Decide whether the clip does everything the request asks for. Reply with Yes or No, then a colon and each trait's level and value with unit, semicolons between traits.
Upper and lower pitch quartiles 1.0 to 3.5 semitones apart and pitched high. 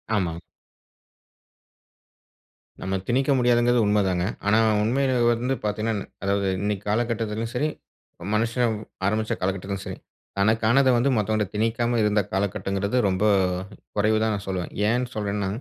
No: average, 2.8 semitones; low, 110 Hz